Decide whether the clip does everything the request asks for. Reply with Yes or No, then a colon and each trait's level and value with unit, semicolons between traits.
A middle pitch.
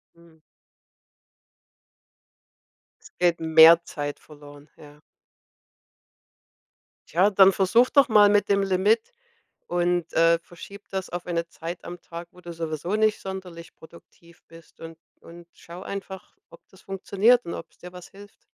Yes: medium, 175 Hz